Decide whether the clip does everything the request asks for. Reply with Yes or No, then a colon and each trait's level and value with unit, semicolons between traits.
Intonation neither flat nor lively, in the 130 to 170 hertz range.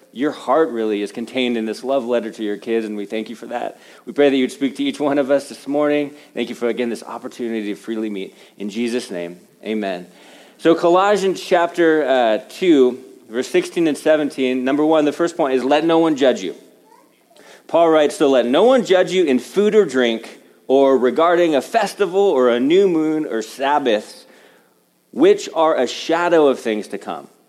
No: wide, 6.1 semitones; medium, 140 Hz